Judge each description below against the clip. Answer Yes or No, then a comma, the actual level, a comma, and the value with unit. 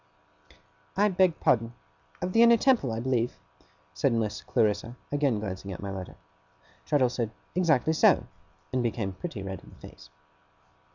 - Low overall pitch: Yes, low, 120 Hz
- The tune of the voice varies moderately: No, wide, 7.3 semitones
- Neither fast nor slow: Yes, average, 155 wpm